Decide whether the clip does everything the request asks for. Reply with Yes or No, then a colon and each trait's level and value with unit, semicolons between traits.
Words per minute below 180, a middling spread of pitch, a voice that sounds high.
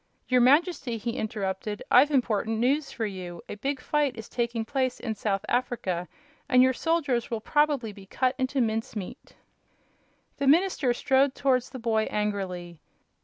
Yes: average, 160 wpm; average, 4.1 semitones; high, 240 Hz